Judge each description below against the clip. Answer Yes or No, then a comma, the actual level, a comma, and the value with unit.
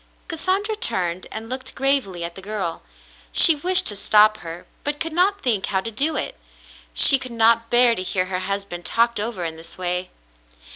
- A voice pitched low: No, high, 220 Hz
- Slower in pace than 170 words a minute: No, average, 195 wpm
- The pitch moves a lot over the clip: Yes, wide, 6.6 semitones